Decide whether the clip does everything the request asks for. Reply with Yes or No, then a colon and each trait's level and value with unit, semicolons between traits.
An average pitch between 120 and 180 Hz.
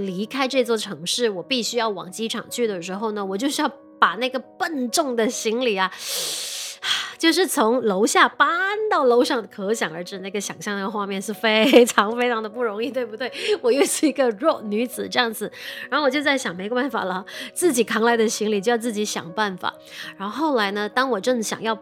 No: high, 230 Hz